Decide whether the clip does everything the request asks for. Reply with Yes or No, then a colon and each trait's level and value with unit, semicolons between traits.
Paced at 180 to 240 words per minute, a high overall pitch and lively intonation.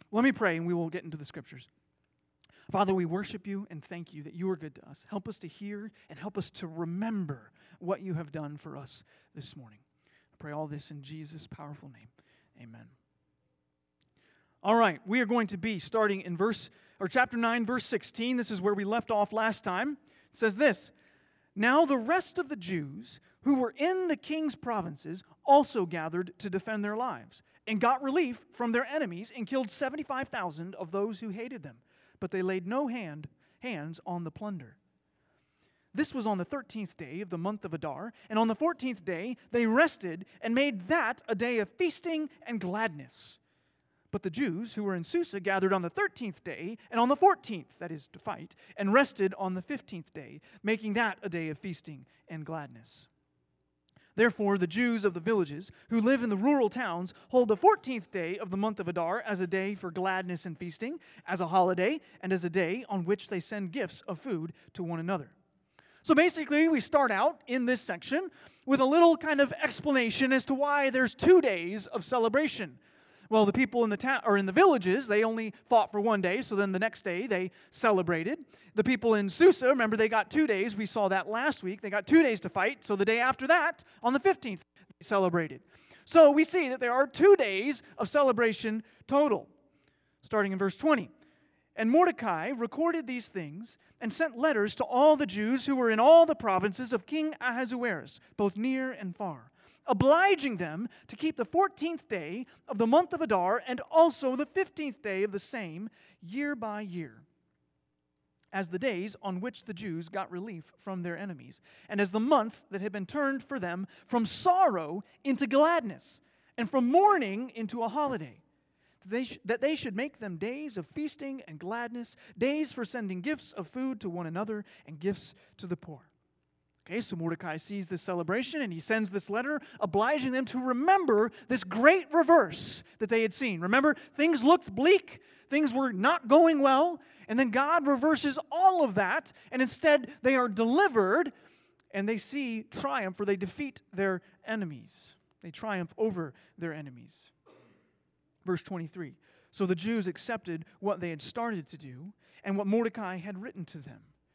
Yes: average, 195 wpm; high, 215 Hz; wide, 6.4 semitones